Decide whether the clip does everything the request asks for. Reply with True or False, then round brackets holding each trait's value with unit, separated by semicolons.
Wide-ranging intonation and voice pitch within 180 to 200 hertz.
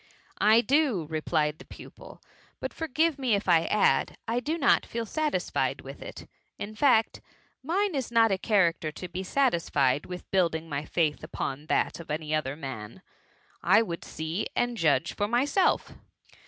True (7.5 semitones; 190 Hz)